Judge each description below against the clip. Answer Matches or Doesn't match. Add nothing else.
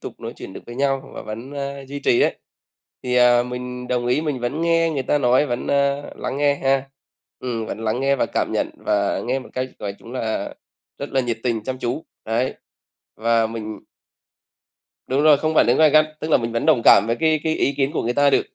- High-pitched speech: Doesn't match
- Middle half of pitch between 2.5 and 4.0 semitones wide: Matches